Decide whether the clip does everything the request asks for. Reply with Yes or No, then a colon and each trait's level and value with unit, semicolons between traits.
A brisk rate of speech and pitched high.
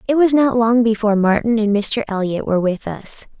Yes: fast, 210 wpm; high, 225 Hz